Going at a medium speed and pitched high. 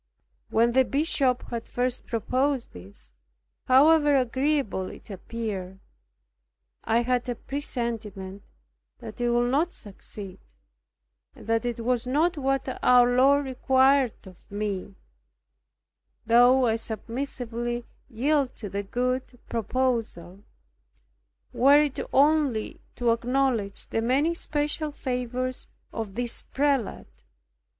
No: slow, 110 wpm; high, 245 Hz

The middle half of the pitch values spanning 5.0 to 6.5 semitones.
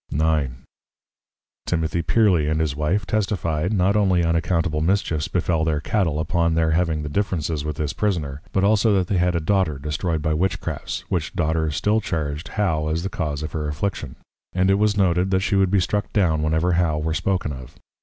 No: average, 3.7 semitones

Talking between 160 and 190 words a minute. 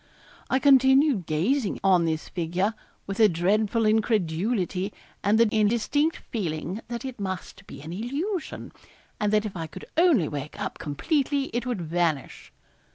No: average, 150 wpm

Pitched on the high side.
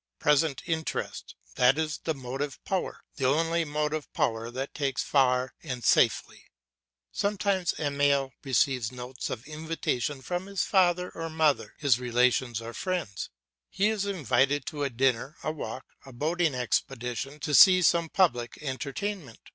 No: medium, 145 Hz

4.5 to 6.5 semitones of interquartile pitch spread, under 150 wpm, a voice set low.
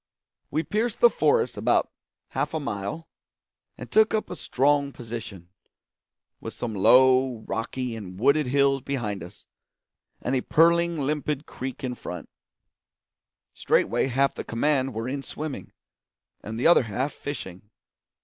Yes: average, 4.8 semitones; average, 140 wpm; low, 130 Hz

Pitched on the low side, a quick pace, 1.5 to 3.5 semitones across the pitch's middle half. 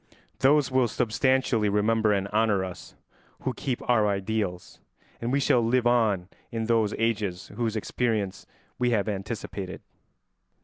No: low, 110 Hz; slow, 135 wpm; average, 3.0 semitones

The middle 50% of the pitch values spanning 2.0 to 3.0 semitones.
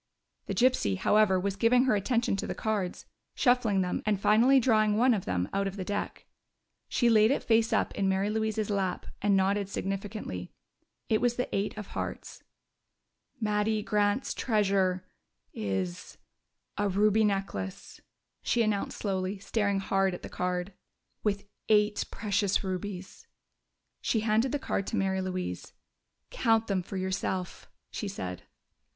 Yes: narrow, 2.4 semitones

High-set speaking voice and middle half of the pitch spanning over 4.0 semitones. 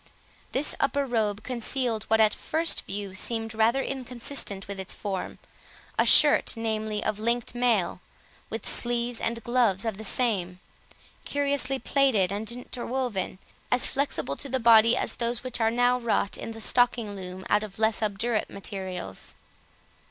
No: high, 225 Hz; average, 3.1 semitones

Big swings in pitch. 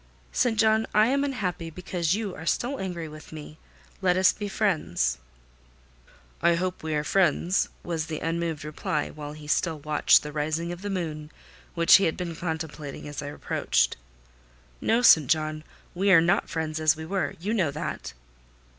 No: average, 3.5 semitones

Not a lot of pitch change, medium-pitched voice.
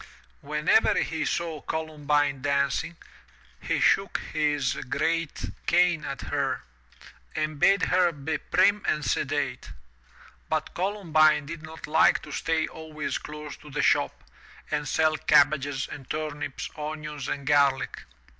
Yes: narrow, 1.8 semitones; medium, 150 Hz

